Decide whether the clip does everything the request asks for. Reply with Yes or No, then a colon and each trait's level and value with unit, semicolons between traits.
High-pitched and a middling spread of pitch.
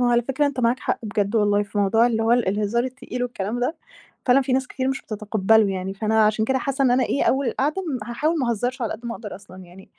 Yes: high, 235 Hz; average, 3.7 semitones